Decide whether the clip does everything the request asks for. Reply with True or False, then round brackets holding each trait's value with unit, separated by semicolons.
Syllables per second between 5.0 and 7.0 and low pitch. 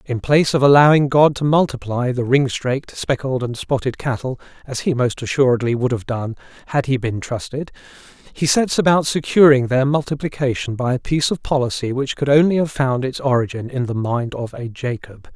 True (5.5 syllables/s; 130 Hz)